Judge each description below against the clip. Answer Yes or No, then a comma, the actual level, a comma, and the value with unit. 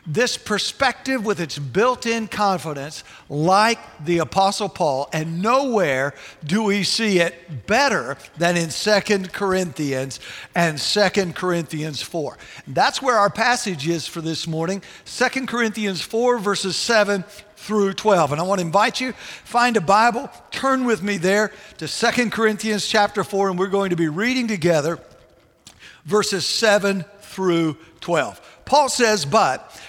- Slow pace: No, average, 145 wpm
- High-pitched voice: Yes, high, 200 Hz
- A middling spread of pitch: Yes, average, 4.3 semitones